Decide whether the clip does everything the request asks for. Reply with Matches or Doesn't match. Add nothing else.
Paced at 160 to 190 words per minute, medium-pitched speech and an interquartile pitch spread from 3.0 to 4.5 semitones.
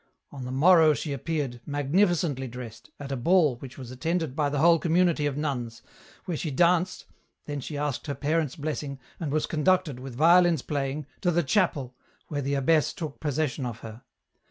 Matches